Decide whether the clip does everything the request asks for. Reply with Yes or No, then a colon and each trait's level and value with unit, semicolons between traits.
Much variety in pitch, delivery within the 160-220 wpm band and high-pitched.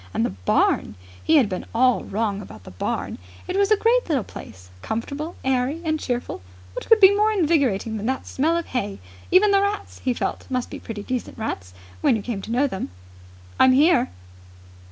Yes: wide, 8.0 semitones; average, 195 wpm; very high, 255 Hz